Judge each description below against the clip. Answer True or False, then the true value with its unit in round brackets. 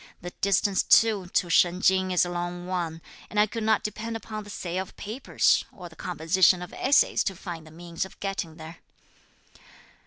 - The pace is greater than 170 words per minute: True (190 wpm)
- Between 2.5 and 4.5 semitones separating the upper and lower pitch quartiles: True (2.9 semitones)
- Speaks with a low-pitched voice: False (185 Hz)